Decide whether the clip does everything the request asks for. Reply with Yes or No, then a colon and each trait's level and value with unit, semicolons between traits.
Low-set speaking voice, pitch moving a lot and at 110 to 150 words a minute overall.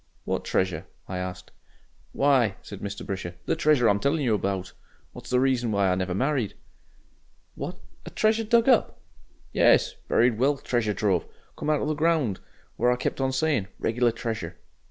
No: low, 120 Hz; wide, 6.2 semitones; average, 175 wpm